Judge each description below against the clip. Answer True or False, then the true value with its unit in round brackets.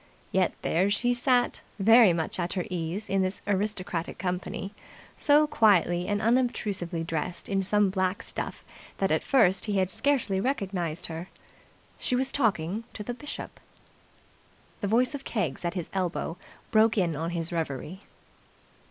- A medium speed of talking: True (150 wpm)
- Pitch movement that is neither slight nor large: True (4.4 semitones)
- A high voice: True (195 Hz)